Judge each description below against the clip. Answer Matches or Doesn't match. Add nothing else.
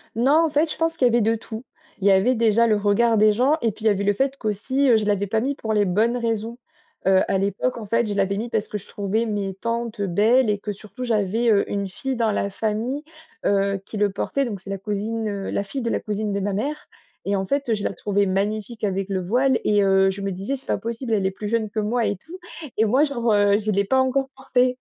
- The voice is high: Matches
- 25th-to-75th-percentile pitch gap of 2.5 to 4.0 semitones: Matches